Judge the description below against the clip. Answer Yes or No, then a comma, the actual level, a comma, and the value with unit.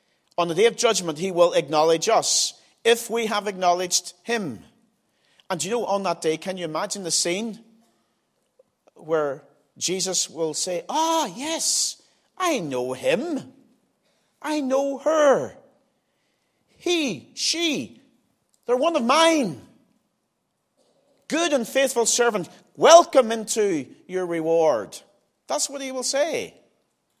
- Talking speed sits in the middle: No, slow, 125 wpm